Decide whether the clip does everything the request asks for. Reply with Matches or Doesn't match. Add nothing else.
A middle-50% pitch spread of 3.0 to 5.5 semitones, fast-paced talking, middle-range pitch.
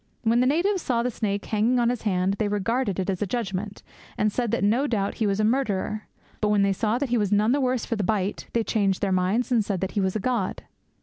Doesn't match